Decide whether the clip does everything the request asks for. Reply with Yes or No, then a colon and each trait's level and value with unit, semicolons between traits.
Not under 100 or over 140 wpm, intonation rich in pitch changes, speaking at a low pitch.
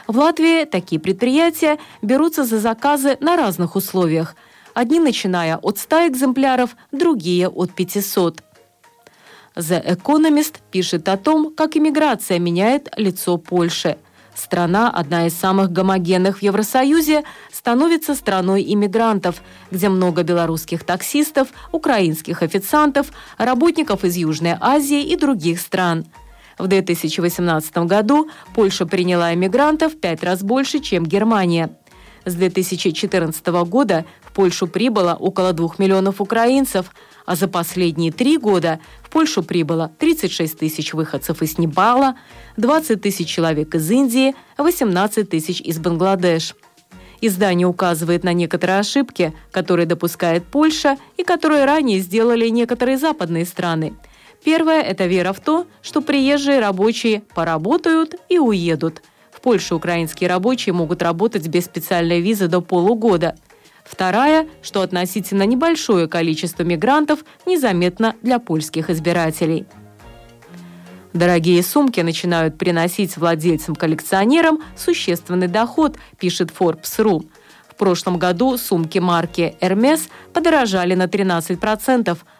No: average, 115 wpm; wide, 7.0 semitones; high, 190 Hz